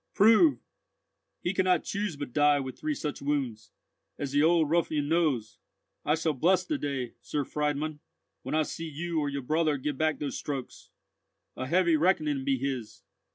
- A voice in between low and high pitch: Yes, medium, 150 Hz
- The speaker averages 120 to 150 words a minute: No, average, 175 wpm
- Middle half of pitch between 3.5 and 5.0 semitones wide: No, average, 3.1 semitones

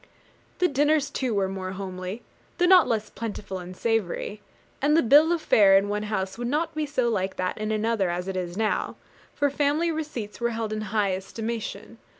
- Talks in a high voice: Yes, high, 220 Hz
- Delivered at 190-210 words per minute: Yes, average, 195 wpm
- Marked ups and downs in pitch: Yes, wide, 6.7 semitones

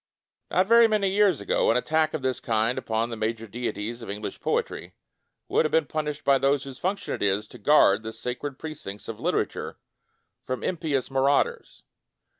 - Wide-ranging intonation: Yes, wide, 5.7 semitones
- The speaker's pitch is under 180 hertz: Yes, low, 135 Hz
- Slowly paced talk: No, average, 190 wpm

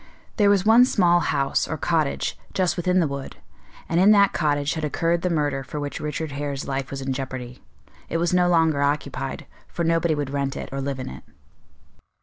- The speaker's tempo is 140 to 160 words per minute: No, average, 200 wpm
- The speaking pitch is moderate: Yes, medium, 150 Hz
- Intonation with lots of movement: No, average, 3.8 semitones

